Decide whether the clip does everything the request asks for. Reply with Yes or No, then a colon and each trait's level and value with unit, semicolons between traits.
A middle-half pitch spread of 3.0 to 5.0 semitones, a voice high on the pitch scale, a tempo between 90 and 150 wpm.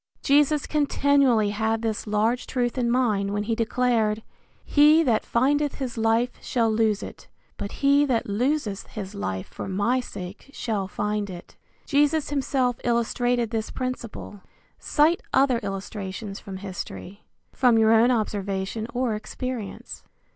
Yes: average, 3.7 semitones; high, 230 Hz; average, 140 wpm